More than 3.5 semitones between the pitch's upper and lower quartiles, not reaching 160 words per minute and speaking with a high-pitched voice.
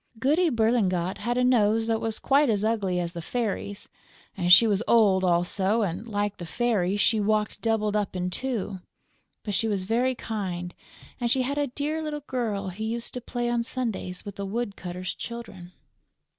No: average, 3.9 semitones; average, 180 wpm; high, 215 Hz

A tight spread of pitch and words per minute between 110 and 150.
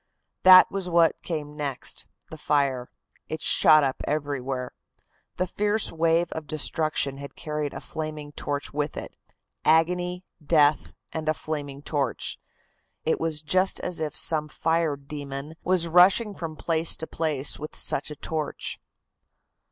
Yes: narrow, 2.3 semitones; average, 145 wpm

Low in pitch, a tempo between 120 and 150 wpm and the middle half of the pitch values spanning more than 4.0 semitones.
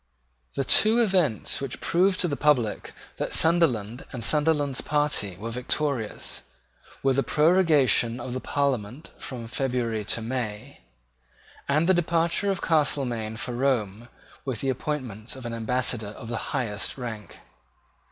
Yes: low, 130 Hz; average, 140 wpm; average, 4.6 semitones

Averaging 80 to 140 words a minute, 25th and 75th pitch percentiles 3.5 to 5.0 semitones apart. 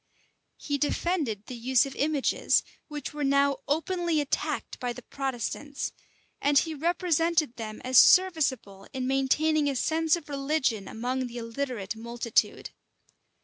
Yes: slow, 135 wpm; average, 4.1 semitones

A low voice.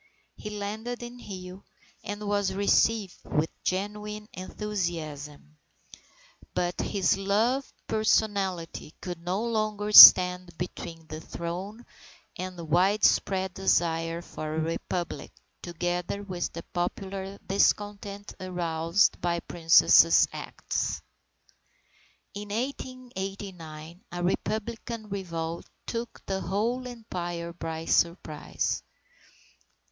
No: high, 190 Hz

